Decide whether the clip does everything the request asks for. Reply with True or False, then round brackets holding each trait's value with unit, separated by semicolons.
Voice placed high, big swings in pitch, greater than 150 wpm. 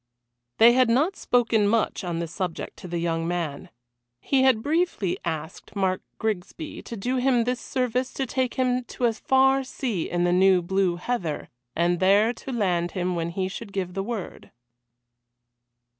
True (205 Hz; 6.0 semitones; 175 wpm)